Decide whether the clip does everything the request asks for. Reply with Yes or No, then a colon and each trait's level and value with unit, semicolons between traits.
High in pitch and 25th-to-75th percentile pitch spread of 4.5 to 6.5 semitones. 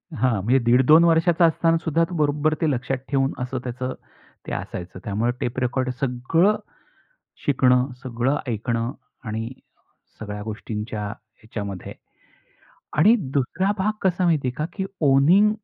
No: low, 130 Hz; wide, 5.5 semitones